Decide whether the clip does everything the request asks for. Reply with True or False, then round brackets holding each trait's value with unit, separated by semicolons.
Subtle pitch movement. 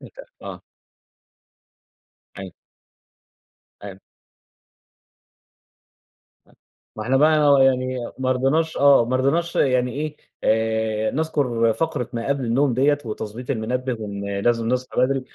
False (3.5 semitones)